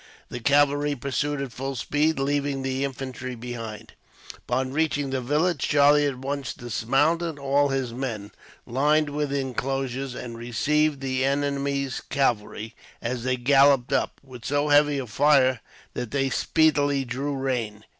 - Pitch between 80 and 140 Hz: Yes, low, 135 Hz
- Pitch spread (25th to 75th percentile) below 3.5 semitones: Yes, narrow, 2.4 semitones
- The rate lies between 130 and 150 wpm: Yes, average, 145 wpm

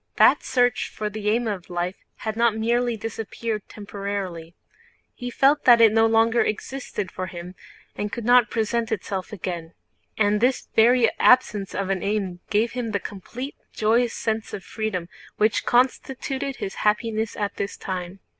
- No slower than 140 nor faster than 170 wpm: Yes, average, 155 wpm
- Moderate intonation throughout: Yes, average, 3.1 semitones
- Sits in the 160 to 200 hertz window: No, high, 215 Hz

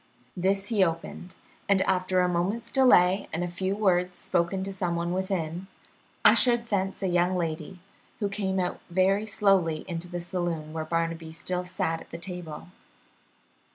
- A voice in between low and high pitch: Yes, medium, 180 Hz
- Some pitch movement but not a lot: No, narrow, 2.1 semitones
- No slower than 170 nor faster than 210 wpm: No, average, 160 wpm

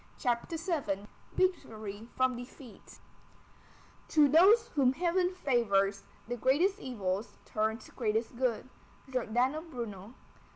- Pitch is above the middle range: Yes, very high, 250 Hz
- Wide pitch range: Yes, wide, 6.2 semitones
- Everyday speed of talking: No, slow, 110 wpm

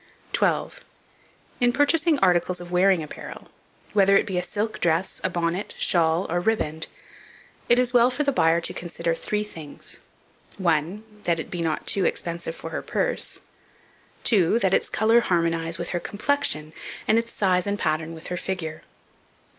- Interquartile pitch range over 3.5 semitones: Yes, average, 4.3 semitones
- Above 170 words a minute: No, average, 165 wpm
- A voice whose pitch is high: No, medium, 180 Hz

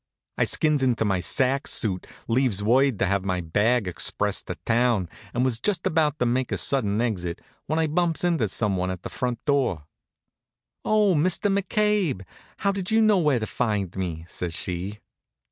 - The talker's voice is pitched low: Yes, low, 120 Hz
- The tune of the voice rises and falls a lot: Yes, wide, 8.0 semitones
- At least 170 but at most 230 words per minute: Yes, average, 180 wpm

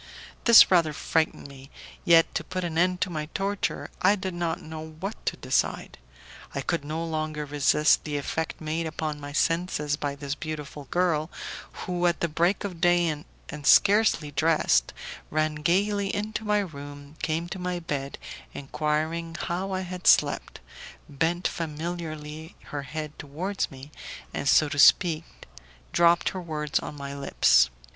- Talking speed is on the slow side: No, average, 155 wpm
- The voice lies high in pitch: No, medium, 160 Hz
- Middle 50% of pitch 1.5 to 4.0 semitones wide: Yes, average, 3.0 semitones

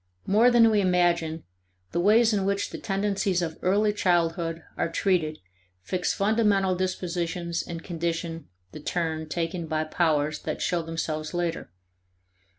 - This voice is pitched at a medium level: Yes, medium, 175 Hz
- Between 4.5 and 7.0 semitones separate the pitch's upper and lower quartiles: No, average, 3.0 semitones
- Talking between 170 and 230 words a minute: No, average, 140 wpm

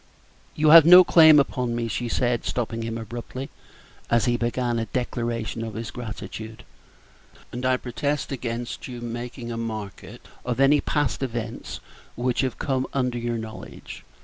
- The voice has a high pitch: No, low, 120 Hz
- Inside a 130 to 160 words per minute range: Yes, average, 155 wpm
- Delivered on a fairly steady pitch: Yes, narrow, 2.0 semitones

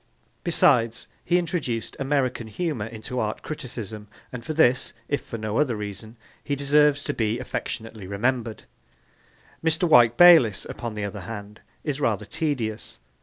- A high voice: No, low, 120 Hz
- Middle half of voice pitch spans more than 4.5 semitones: Yes, average, 5.1 semitones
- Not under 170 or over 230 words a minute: No, average, 145 wpm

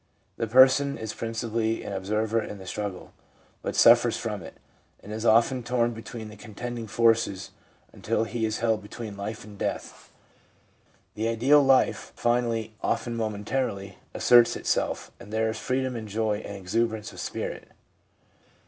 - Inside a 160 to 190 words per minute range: No, average, 150 wpm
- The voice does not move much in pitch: Yes, narrow, 1.9 semitones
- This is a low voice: Yes, low, 110 Hz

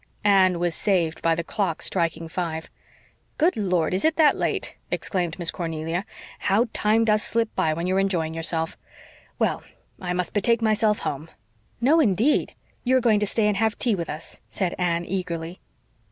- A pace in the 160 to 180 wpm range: Yes, average, 170 wpm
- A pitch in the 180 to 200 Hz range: Yes, medium, 185 Hz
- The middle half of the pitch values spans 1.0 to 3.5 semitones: No, average, 4.2 semitones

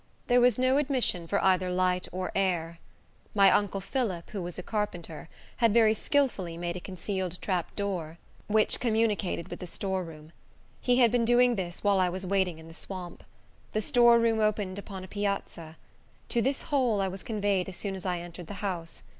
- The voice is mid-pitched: No, high, 195 Hz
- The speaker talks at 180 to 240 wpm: Yes, average, 190 wpm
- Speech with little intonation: No, average, 3.7 semitones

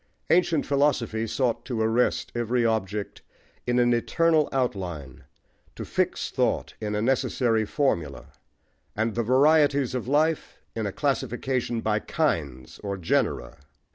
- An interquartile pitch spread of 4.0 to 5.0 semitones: Yes, average, 4.5 semitones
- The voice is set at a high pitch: No, low, 120 Hz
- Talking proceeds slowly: Yes, slow, 130 wpm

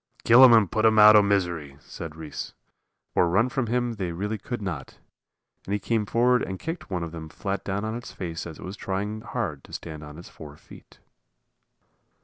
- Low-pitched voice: Yes, low, 100 Hz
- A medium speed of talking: No, fast, 210 wpm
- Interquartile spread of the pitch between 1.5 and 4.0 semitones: No, average, 4.9 semitones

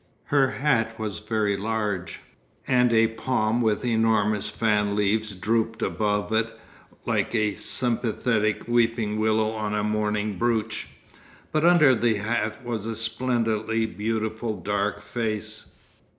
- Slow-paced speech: Yes, slow, 125 wpm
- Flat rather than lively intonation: Yes, narrow, 1.5 semitones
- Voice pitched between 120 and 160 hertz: No, low, 110 Hz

